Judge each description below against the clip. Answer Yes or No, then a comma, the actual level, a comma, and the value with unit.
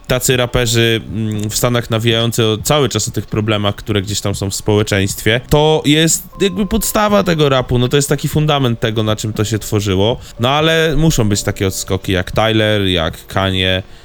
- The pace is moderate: No, fast, 190 wpm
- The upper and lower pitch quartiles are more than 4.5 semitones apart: Yes, wide, 5.6 semitones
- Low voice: Yes, low, 115 Hz